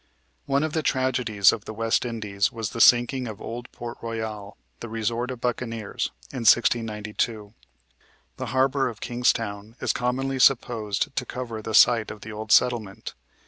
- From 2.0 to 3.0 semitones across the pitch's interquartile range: Yes, narrow, 2.4 semitones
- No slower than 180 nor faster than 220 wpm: No, average, 160 wpm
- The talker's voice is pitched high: No, low, 115 Hz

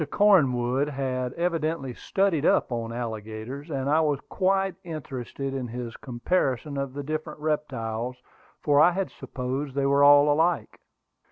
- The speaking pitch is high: No, medium, 140 Hz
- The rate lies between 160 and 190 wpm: No, average, 145 wpm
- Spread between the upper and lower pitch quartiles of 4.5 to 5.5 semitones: No, average, 3.7 semitones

